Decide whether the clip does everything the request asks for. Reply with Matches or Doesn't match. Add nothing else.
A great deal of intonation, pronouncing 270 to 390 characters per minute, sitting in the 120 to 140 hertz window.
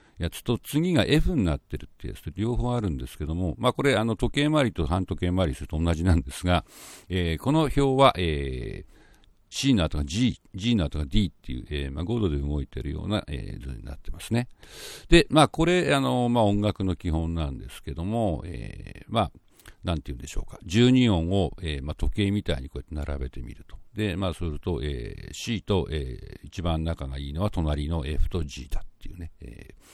Doesn't match